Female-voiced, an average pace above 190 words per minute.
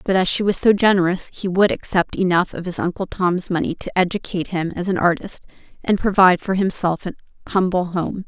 Yes: female; fast, 205 wpm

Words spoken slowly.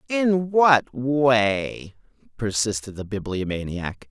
Yes: slow, 90 wpm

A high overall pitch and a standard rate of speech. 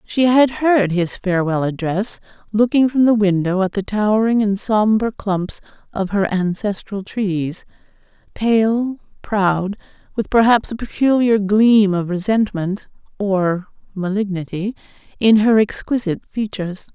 No: high, 205 Hz; slow, 115 wpm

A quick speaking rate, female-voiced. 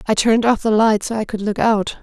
Yes: fast, 295 wpm; female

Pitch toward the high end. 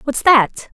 Yes: very high, 265 Hz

